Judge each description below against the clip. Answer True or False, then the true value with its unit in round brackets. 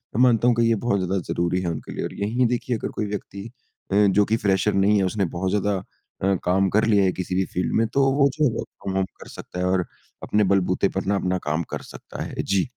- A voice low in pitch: True (100 Hz)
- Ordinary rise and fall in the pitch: True (3.2 semitones)